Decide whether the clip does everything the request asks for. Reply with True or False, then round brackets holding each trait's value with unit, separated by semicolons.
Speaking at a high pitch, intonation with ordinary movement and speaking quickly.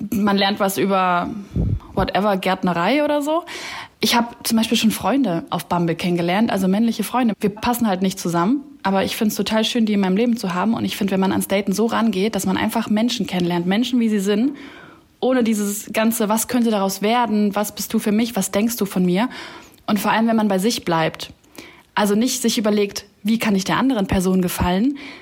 True (210 Hz; 3.3 semitones; 215 wpm)